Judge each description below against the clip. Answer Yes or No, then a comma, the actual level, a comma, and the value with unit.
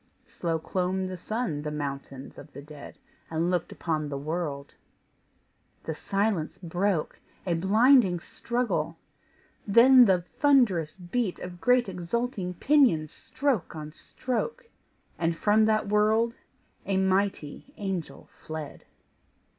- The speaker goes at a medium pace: No, slow, 120 wpm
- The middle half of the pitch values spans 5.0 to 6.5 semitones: Yes, wide, 5.5 semitones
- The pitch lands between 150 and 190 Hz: Yes, medium, 185 Hz